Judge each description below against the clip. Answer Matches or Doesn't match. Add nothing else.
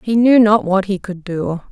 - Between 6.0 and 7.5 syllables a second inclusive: Doesn't match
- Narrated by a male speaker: Doesn't match